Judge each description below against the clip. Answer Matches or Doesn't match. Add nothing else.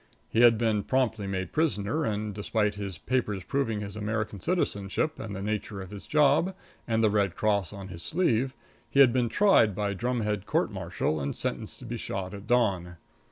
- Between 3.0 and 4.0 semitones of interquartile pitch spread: Matches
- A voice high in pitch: Doesn't match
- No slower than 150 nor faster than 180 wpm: Doesn't match